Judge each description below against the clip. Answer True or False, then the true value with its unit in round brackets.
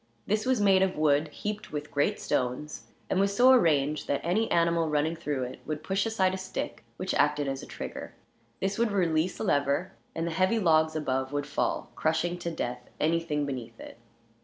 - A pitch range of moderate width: True (4.6 semitones)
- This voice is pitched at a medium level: True (160 Hz)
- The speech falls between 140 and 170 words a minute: False (195 wpm)